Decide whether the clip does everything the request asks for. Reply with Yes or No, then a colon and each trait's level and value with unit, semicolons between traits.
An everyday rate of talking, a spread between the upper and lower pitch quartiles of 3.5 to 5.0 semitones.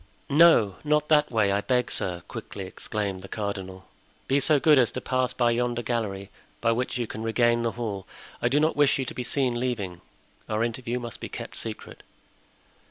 Yes: average, 195 wpm; average, 3.9 semitones